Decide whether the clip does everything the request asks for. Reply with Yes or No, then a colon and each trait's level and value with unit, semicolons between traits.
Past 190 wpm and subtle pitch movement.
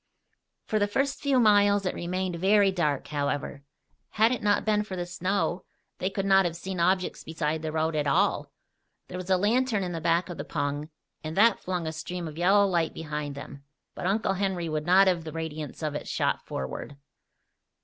No: average, 200 wpm; average, 3.9 semitones